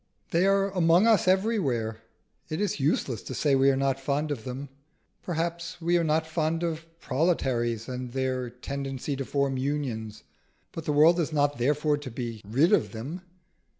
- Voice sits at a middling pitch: Yes, medium, 145 Hz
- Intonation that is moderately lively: Yes, average, 4.4 semitones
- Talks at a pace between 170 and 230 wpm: Yes, average, 175 wpm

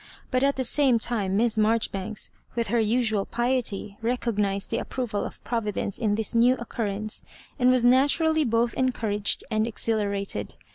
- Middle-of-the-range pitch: No, high, 230 Hz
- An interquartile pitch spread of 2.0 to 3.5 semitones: Yes, average, 2.9 semitones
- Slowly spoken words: No, average, 155 wpm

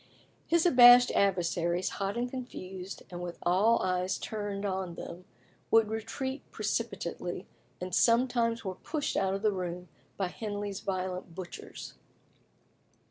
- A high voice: Yes, high, 195 Hz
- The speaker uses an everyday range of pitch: Yes, average, 4.1 semitones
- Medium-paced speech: No, slow, 130 wpm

